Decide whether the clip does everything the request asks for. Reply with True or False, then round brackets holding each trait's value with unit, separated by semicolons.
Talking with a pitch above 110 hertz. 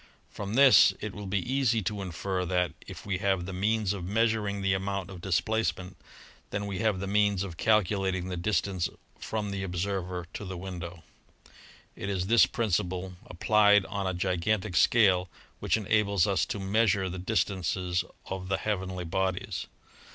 False (95 Hz)